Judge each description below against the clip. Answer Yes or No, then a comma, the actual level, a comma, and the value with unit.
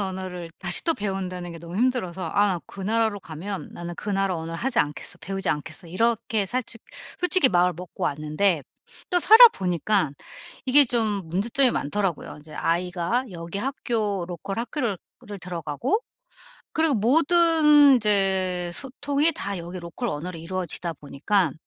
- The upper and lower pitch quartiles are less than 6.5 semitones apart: Yes, wide, 5.4 semitones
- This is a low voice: No, high, 195 Hz